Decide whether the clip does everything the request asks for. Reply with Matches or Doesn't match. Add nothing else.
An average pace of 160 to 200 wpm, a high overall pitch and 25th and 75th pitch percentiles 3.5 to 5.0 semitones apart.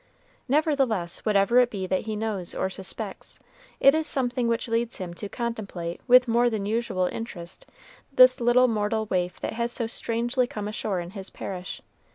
Matches